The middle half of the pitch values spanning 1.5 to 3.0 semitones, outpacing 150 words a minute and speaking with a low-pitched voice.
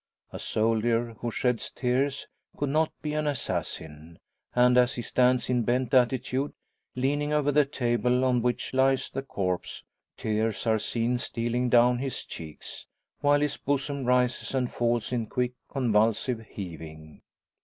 No: average, 2.7 semitones; average, 145 wpm; low, 125 Hz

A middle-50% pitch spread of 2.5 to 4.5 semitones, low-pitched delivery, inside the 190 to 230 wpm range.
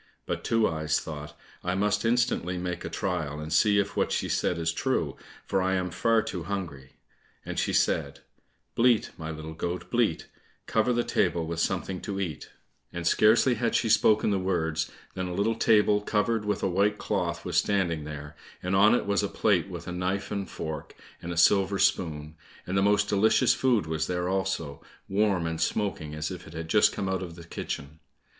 Yes: average, 4.1 semitones; very low, 95 Hz; average, 200 wpm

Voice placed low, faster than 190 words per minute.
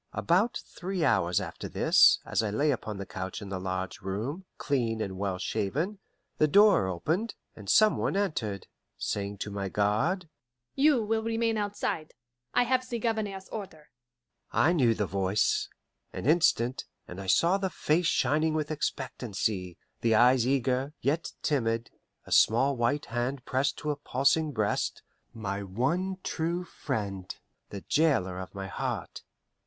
No: low, 130 Hz; average, 155 wpm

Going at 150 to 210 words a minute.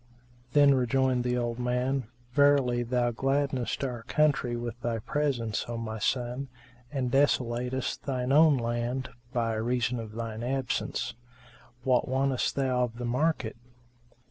No: average, 140 wpm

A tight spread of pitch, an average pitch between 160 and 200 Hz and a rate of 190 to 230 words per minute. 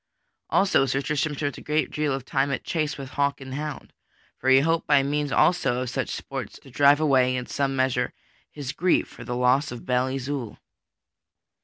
No: narrow, 2.3 semitones; low, 135 Hz; average, 195 wpm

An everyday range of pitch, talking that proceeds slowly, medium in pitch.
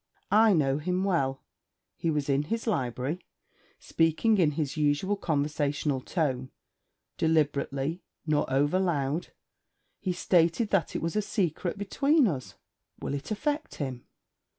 Yes: average, 5.0 semitones; slow, 130 wpm; medium, 160 Hz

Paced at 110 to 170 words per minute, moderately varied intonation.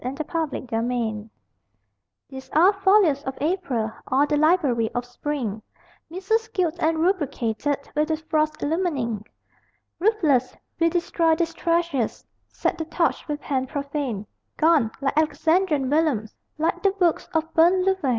Yes: average, 140 wpm; average, 4.5 semitones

